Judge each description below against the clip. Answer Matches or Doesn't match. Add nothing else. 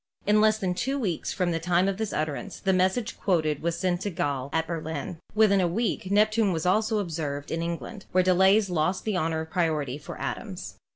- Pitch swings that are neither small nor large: Matches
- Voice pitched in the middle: Matches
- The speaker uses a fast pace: Matches